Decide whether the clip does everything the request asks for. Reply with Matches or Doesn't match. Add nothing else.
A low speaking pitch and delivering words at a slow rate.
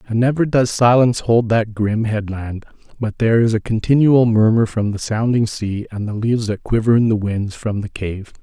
Doesn't match